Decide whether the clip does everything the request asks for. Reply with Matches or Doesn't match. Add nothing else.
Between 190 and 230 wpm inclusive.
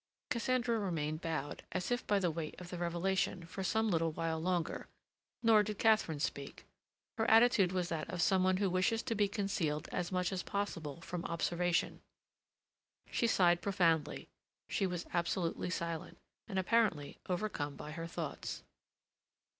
Doesn't match